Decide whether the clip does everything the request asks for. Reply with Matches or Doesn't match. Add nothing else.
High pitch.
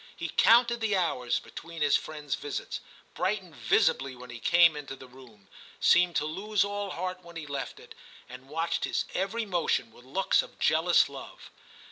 Doesn't match